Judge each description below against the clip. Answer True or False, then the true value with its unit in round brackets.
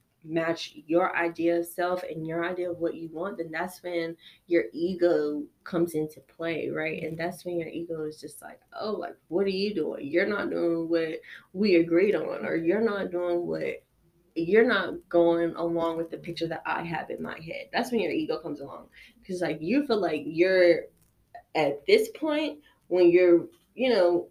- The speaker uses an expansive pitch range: False (3.0 semitones)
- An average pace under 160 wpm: False (195 wpm)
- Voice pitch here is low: False (170 Hz)